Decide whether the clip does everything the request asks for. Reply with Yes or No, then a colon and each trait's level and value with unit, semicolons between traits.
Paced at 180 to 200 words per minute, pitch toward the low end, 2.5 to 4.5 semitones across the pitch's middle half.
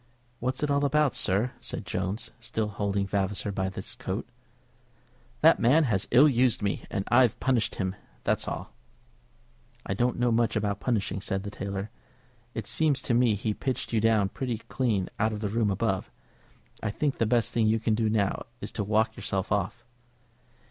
Yes: average, 185 wpm; low, 110 Hz; average, 3.4 semitones